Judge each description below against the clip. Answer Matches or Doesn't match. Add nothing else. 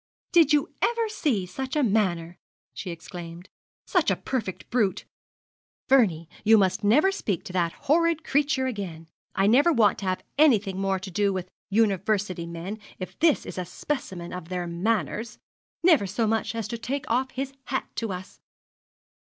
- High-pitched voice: Matches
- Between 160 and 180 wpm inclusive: Matches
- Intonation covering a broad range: Matches